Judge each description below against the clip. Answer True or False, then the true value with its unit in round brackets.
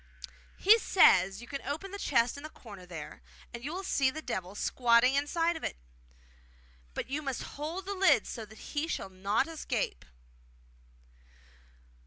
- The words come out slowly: False (160 wpm)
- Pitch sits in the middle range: False (275 Hz)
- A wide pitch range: True (6.8 semitones)